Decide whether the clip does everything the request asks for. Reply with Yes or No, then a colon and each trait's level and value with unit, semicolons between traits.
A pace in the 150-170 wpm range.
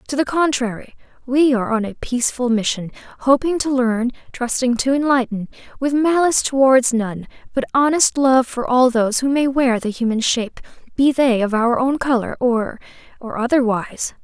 Yes: average, 160 wpm